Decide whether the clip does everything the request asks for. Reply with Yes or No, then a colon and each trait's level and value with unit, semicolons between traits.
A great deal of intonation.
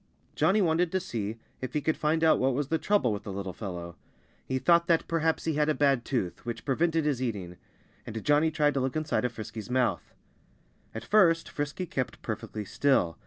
Yes: wide, 6.0 semitones